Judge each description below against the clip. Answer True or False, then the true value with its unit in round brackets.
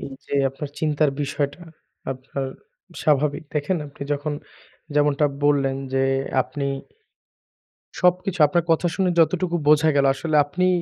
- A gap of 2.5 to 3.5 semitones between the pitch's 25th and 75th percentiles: True (2.8 semitones)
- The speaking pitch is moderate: True (150 Hz)